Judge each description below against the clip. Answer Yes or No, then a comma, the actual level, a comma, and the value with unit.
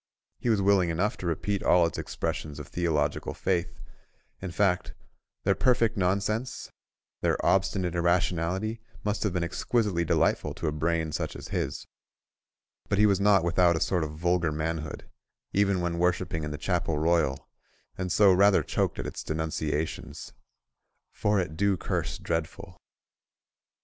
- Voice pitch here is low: Yes, very low, 90 Hz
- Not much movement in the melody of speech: No, average, 3.3 semitones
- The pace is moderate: Yes, average, 145 wpm